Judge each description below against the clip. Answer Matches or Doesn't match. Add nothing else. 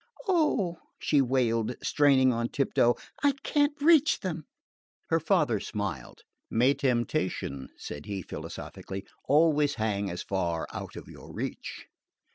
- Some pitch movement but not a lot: Doesn't match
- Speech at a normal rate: Doesn't match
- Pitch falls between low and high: Doesn't match